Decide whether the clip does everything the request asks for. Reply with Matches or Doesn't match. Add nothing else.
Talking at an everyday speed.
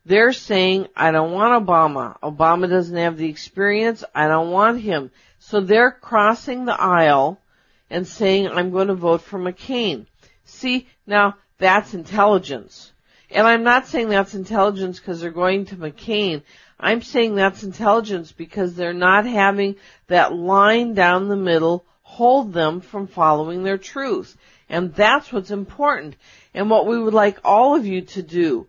Matches